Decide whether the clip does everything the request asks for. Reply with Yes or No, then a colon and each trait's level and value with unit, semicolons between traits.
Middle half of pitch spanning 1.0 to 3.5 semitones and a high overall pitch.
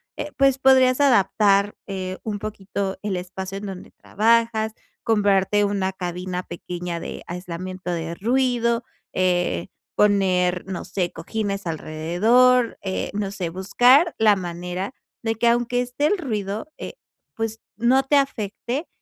No: average, 4.3 semitones; high, 200 Hz